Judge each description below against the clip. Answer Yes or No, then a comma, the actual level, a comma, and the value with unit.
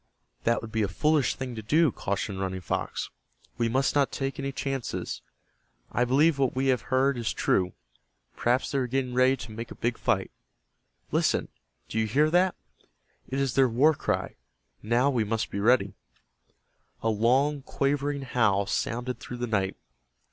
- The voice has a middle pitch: No, low, 125 Hz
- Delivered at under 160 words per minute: No, average, 170 wpm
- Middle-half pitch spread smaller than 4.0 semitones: Yes, average, 3.5 semitones